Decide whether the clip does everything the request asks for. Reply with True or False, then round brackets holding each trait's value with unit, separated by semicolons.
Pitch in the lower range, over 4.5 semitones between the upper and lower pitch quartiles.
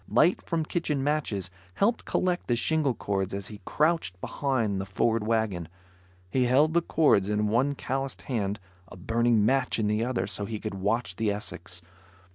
True (115 Hz; 5.3 semitones)